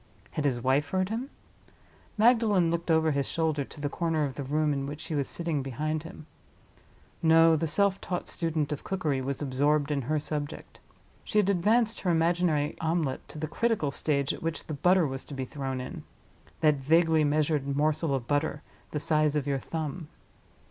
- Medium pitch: Yes, medium, 155 Hz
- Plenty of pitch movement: No, average, 2.7 semitones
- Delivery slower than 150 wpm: No, average, 185 wpm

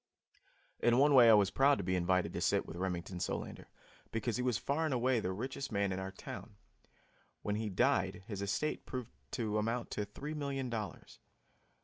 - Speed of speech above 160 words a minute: Yes, average, 195 wpm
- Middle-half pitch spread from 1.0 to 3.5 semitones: No, average, 4.9 semitones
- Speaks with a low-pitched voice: Yes, low, 110 Hz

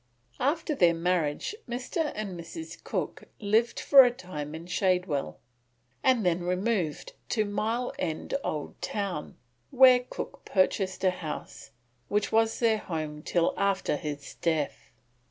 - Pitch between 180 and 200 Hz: Yes, high, 190 Hz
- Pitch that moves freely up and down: Yes, wide, 5.7 semitones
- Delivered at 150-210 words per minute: No, slow, 135 wpm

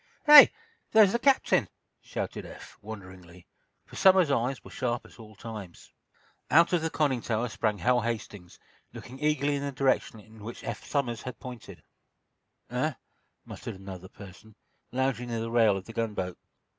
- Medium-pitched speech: No, low, 115 Hz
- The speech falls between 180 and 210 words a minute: No, average, 155 wpm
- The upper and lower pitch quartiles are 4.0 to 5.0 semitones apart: Yes, average, 4.7 semitones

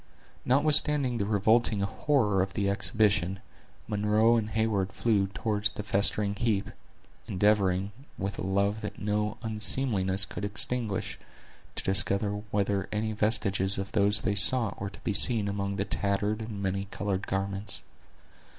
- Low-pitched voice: Yes, low, 100 Hz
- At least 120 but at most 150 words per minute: Yes, average, 140 wpm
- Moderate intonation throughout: No, narrow, 1.8 semitones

